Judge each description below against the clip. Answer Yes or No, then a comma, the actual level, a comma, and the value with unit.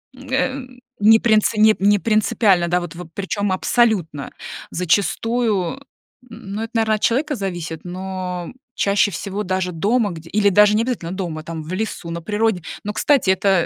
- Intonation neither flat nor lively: Yes, average, 3.7 semitones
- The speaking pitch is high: Yes, high, 200 Hz